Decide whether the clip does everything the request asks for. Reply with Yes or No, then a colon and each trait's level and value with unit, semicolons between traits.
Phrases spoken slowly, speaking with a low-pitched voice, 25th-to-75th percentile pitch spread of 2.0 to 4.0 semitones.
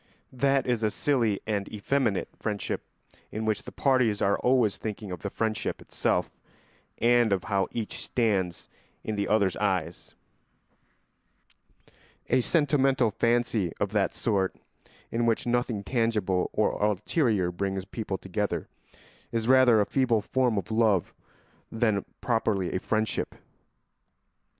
Yes: slow, 130 wpm; low, 110 Hz; average, 3.3 semitones